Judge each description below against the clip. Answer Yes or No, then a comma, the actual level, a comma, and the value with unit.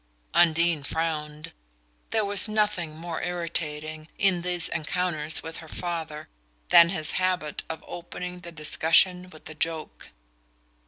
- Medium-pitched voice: Yes, medium, 165 Hz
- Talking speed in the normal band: No, slow, 125 wpm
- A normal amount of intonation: No, narrow, 2.3 semitones